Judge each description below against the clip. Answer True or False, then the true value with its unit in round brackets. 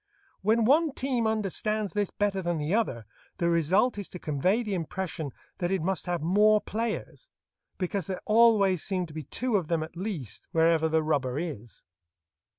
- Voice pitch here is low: False (185 Hz)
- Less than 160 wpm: False (175 wpm)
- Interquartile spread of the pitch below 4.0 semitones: False (4.8 semitones)